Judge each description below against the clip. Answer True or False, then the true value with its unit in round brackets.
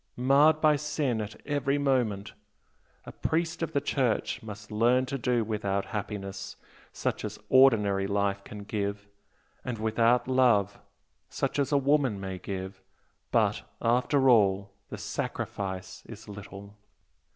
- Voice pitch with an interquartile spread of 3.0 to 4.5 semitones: False (5.0 semitones)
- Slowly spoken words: True (130 wpm)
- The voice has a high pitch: False (110 Hz)